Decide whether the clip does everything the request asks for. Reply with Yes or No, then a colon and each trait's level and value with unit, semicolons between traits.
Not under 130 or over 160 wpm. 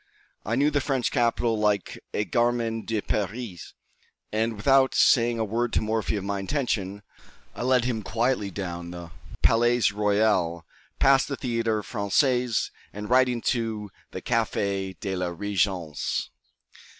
Yes: average, 140 wpm